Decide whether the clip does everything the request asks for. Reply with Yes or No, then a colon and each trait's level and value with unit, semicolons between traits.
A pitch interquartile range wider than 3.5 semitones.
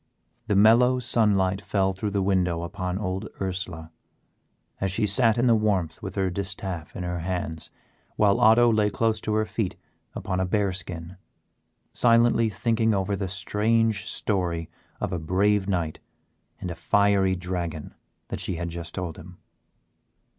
No: average, 3.0 semitones